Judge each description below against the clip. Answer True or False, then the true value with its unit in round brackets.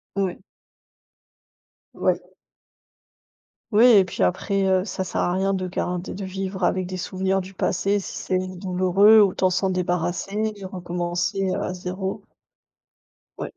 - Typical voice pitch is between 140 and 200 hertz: True (185 Hz)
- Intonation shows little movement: True (1.3 semitones)